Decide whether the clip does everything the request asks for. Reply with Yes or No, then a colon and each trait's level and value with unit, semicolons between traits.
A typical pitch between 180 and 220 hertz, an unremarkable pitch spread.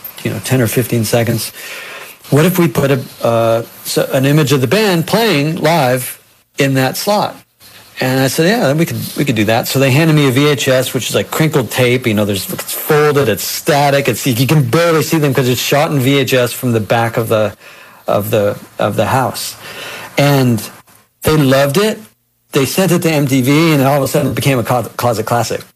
No: low, 135 Hz; average, 3.9 semitones